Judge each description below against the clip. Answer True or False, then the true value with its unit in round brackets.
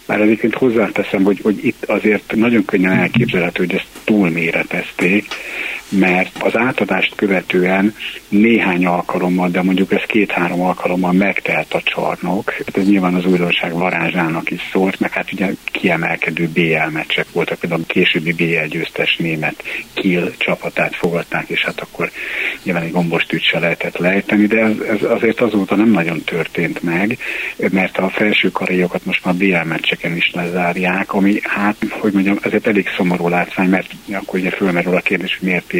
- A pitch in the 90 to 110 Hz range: True (95 Hz)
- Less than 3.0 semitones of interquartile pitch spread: True (2.4 semitones)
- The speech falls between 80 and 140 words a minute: False (155 wpm)